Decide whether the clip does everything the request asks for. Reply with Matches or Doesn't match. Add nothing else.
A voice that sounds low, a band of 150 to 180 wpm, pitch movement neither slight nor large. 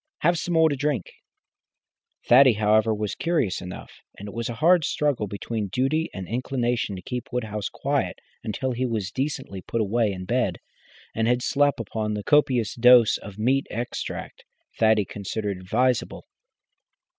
Matches